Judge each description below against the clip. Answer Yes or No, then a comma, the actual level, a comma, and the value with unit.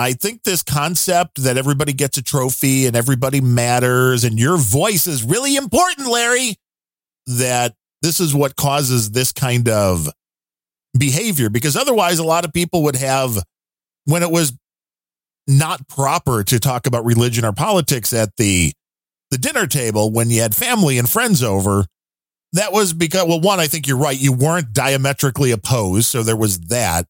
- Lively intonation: Yes, wide, 6.0 semitones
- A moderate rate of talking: Yes, average, 170 wpm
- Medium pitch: No, low, 130 Hz